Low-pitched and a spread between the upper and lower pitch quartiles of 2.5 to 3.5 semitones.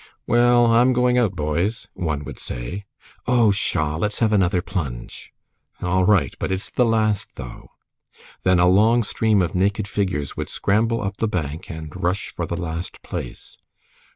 No: very low, 95 Hz; average, 4.8 semitones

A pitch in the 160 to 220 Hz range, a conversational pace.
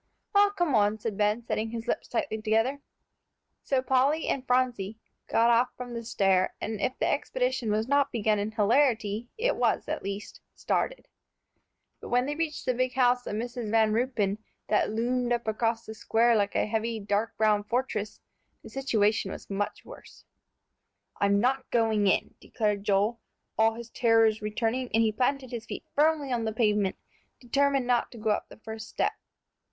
No: high, 230 Hz; average, 180 wpm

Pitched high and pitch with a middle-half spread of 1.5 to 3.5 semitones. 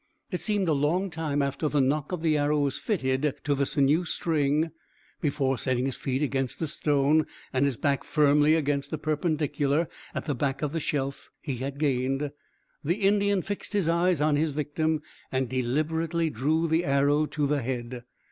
No: medium, 145 Hz; narrow, 2.6 semitones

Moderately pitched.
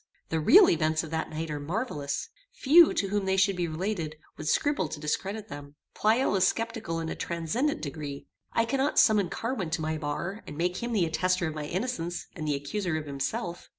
Yes: medium, 175 Hz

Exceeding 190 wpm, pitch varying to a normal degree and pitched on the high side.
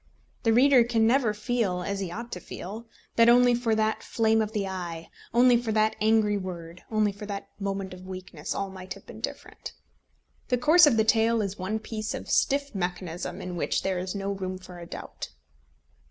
Yes: average, 200 wpm; average, 3.7 semitones; high, 210 Hz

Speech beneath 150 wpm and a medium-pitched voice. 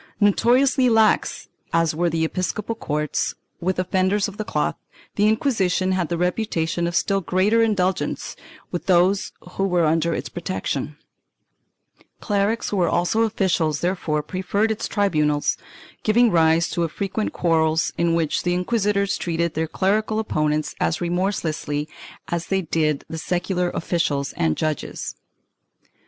Yes: average, 140 wpm; medium, 180 Hz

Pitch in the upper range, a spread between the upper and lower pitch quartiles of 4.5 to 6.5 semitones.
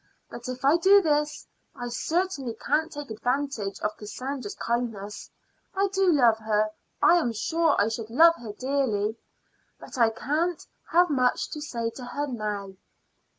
Yes: very high, 255 Hz; wide, 5.4 semitones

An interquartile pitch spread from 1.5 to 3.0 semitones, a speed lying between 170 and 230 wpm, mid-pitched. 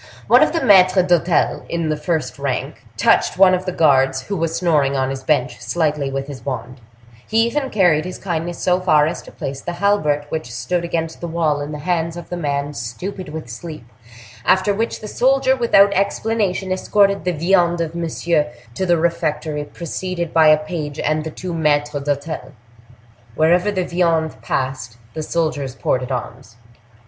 No: average, 3.9 semitones; average, 180 wpm; medium, 160 Hz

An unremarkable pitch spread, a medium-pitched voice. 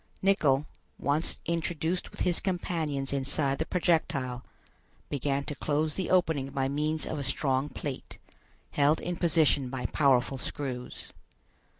Yes: average, 3.0 semitones; medium, 145 Hz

